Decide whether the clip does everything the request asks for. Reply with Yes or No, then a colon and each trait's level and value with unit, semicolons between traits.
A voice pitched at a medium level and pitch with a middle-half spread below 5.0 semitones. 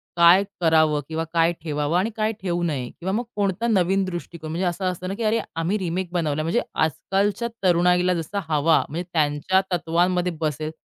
Yes: medium, 175 Hz; average, 2.8 semitones